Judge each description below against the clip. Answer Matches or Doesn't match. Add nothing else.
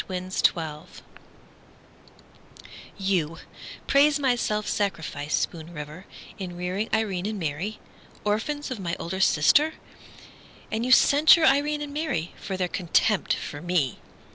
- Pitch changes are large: Matches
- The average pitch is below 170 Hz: Doesn't match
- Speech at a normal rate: Doesn't match